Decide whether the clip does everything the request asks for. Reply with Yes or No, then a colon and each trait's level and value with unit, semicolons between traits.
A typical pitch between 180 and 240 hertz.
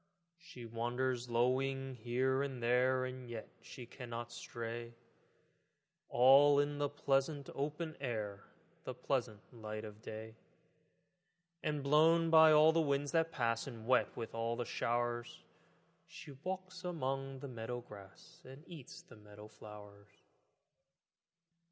No: low, 125 Hz